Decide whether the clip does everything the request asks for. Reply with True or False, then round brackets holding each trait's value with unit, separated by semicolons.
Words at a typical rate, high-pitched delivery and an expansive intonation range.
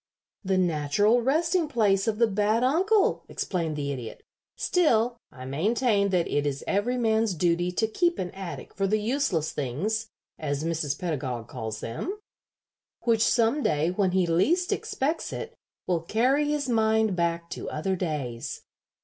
True (155 wpm; 195 Hz; 6.4 semitones)